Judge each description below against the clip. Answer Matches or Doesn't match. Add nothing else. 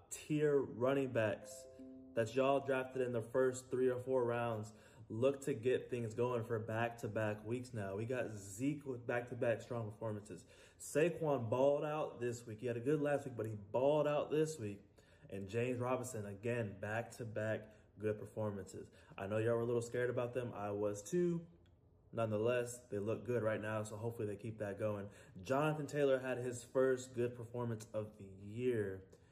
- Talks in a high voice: Doesn't match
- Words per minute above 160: Matches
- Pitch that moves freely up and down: Doesn't match